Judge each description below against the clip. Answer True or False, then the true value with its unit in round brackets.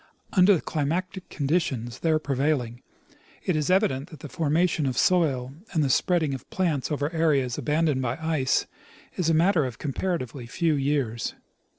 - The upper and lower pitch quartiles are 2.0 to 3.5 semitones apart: False (4.0 semitones)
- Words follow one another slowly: False (160 wpm)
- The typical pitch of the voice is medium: True (150 Hz)